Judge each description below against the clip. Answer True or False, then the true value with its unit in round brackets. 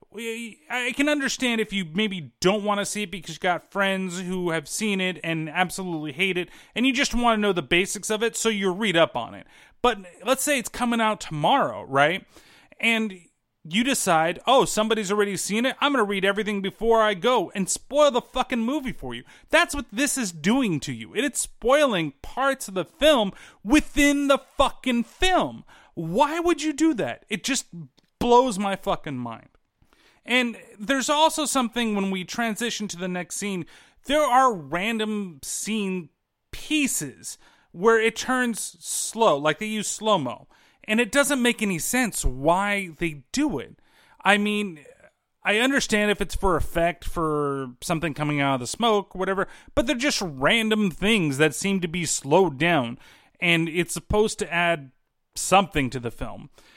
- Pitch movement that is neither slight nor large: False (6.0 semitones)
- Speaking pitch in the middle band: False (205 Hz)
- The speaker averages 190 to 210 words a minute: False (180 wpm)